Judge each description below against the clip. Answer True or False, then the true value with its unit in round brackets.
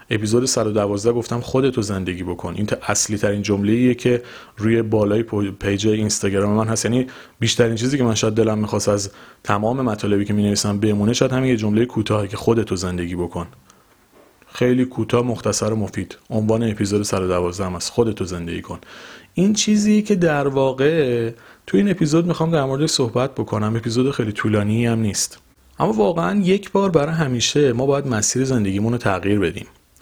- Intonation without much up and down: False (3.8 semitones)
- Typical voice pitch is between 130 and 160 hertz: False (110 Hz)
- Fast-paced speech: True (170 wpm)